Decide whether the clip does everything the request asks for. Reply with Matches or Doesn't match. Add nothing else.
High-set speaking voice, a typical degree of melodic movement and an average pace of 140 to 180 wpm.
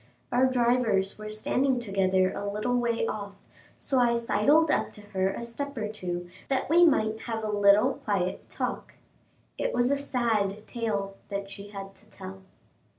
Matches